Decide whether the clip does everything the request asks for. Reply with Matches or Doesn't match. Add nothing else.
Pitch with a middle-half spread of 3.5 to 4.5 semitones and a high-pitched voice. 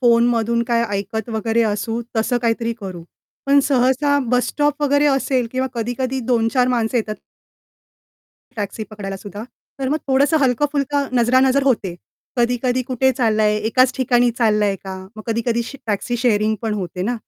Doesn't match